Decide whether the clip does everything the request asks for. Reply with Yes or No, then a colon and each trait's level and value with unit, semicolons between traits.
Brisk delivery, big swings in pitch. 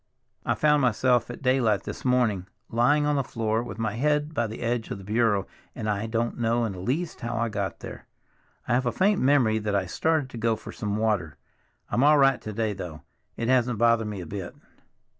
No: fast, 220 wpm; average, 3.3 semitones